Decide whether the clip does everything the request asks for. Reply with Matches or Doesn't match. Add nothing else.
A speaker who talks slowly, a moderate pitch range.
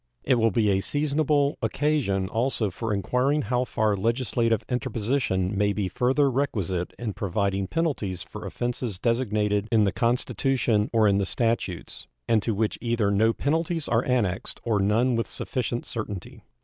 Doesn't match